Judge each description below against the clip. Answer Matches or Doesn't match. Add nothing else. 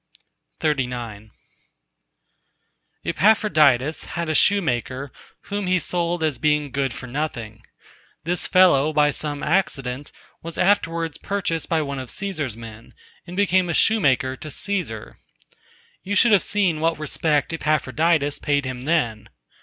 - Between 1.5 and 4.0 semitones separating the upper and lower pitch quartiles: Doesn't match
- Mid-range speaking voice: Matches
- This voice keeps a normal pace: Doesn't match